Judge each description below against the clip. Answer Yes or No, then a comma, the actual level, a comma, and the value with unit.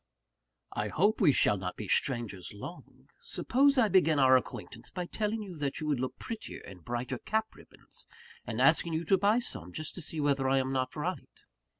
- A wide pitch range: Yes, wide, 7.5 semitones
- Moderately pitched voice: Yes, medium, 150 Hz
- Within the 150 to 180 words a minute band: No, average, 200 wpm